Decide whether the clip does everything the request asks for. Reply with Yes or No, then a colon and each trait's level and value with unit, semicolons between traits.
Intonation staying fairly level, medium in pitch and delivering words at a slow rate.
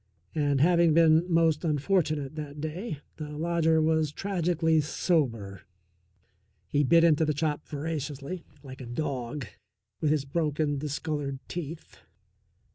Yes: narrow, 2.2 semitones; medium, 155 Hz; slow, 120 wpm